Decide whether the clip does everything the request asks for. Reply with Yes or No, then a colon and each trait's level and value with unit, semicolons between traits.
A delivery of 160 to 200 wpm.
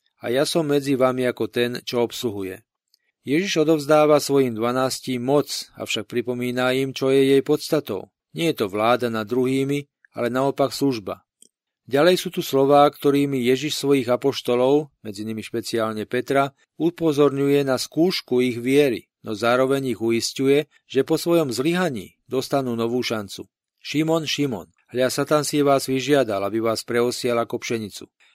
No: average, 150 wpm